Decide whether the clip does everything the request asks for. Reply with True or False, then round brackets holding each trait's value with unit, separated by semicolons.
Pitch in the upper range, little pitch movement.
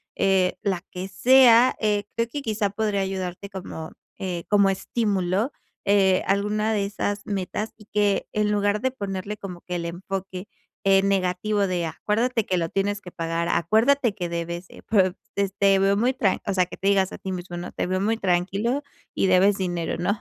True (195 Hz; 2.3 semitones)